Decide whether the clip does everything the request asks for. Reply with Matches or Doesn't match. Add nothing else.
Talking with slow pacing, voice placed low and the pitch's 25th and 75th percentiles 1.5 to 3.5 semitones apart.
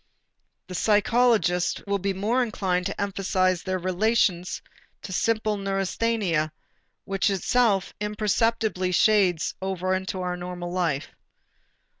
Doesn't match